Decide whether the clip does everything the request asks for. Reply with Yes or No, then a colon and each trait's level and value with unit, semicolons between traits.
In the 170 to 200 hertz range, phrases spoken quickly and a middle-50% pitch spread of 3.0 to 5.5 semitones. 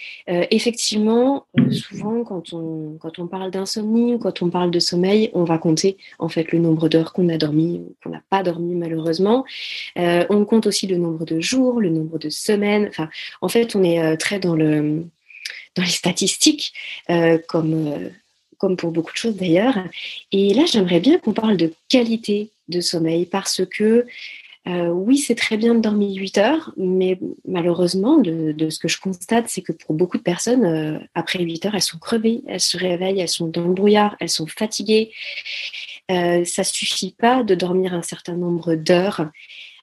No: medium, 185 Hz; average, 195 wpm; average, 4.4 semitones